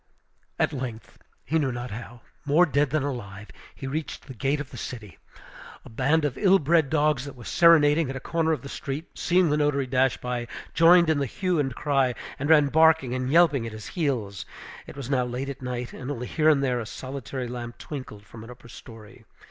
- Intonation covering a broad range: No, average, 3.6 semitones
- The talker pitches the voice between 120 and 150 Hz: Yes, low, 135 Hz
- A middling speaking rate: No, fast, 215 wpm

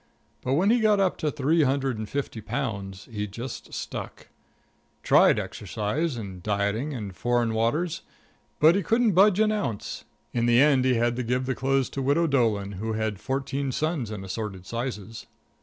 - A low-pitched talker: Yes, low, 125 Hz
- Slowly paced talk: No, average, 180 wpm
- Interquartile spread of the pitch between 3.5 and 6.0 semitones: Yes, wide, 5.4 semitones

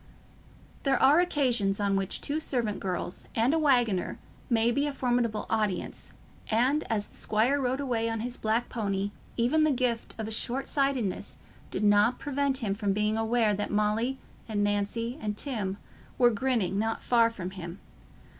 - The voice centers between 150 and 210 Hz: No, high, 230 Hz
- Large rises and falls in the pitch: No, average, 3.8 semitones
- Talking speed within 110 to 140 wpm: No, average, 165 wpm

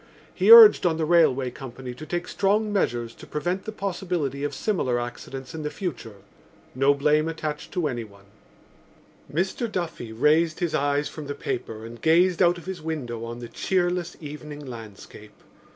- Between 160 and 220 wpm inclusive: Yes, average, 170 wpm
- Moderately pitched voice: Yes, medium, 150 Hz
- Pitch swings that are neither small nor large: No, wide, 5.8 semitones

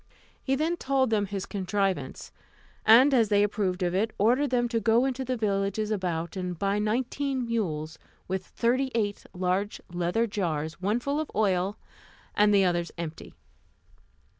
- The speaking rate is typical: Yes, average, 160 wpm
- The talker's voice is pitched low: No, high, 205 Hz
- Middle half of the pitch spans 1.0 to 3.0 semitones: No, average, 4.4 semitones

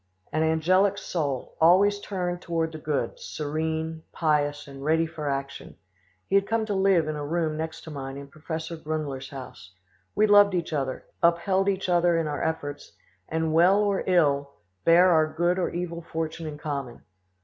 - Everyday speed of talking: Yes, average, 175 wpm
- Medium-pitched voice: Yes, medium, 160 Hz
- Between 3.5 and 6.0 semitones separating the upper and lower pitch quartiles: No, average, 3.0 semitones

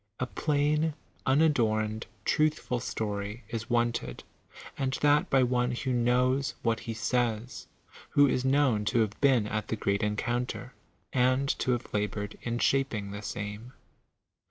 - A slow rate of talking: No, average, 145 wpm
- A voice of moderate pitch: No, low, 120 Hz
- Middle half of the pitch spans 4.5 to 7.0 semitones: No, average, 3.5 semitones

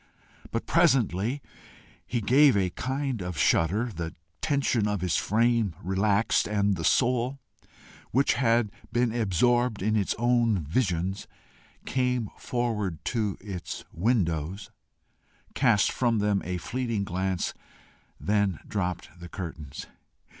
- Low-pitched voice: Yes, low, 105 Hz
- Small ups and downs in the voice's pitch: No, average, 4.6 semitones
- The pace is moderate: No, slow, 120 wpm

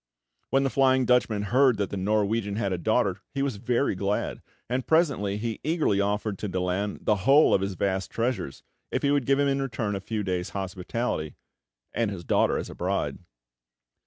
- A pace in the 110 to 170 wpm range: No, average, 190 wpm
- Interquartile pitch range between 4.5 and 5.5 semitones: Yes, average, 4.8 semitones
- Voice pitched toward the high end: No, low, 105 Hz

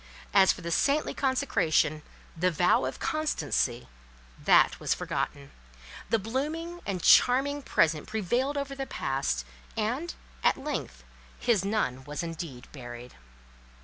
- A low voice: No, high, 195 Hz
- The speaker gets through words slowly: Yes, slow, 125 wpm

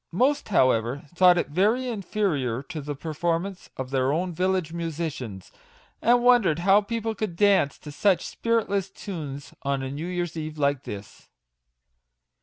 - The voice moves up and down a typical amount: No, wide, 5.8 semitones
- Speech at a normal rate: Yes, average, 150 wpm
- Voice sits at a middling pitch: Yes, medium, 170 Hz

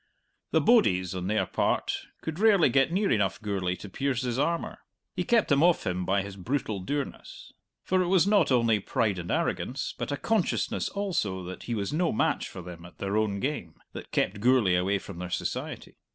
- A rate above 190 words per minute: Yes, average, 200 wpm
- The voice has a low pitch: Yes, low, 110 Hz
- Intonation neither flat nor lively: No, wide, 9.0 semitones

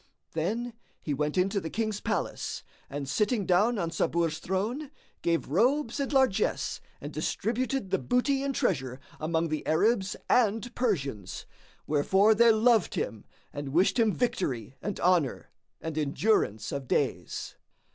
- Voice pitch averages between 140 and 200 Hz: Yes, high, 190 Hz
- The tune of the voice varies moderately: No, wide, 7.0 semitones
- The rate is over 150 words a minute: No, average, 140 wpm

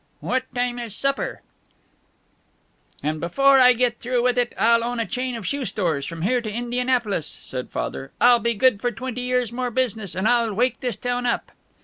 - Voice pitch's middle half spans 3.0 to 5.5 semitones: No, narrow, 2.5 semitones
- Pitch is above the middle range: Yes, high, 240 Hz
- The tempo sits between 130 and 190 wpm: No, average, 200 wpm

